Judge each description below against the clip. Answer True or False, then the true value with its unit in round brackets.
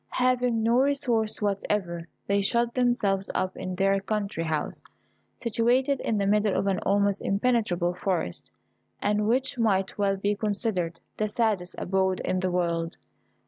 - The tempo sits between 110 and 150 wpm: True (145 wpm)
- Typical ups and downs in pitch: True (3.5 semitones)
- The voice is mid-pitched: False (205 Hz)